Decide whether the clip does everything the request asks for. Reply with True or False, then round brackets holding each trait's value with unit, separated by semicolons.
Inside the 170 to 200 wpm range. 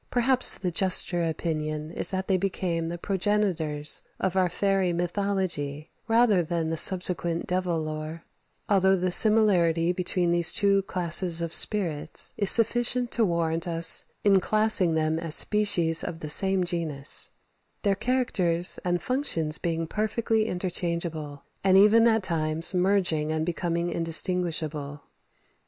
False (135 wpm)